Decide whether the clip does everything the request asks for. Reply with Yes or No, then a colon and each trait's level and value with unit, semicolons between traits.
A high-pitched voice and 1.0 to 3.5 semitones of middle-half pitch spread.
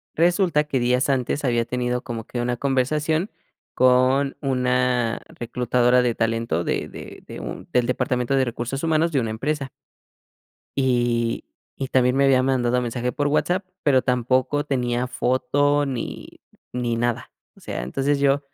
No: low, 125 Hz; narrow, 2.4 semitones